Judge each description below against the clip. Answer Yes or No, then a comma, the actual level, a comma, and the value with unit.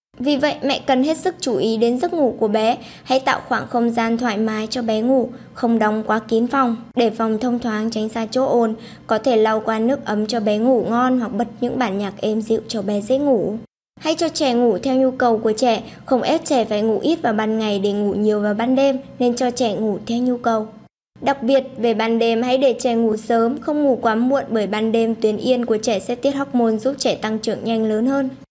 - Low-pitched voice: No, high, 235 Hz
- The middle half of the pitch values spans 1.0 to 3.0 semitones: Yes, average, 2.7 semitones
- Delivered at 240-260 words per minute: Yes, fast, 250 wpm